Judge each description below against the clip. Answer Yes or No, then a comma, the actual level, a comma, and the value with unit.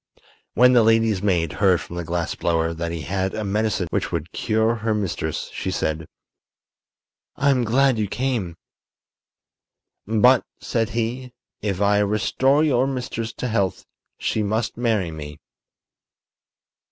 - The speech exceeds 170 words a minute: No, average, 140 wpm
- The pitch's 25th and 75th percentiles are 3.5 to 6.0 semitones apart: Yes, average, 4.5 semitones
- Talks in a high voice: No, low, 110 Hz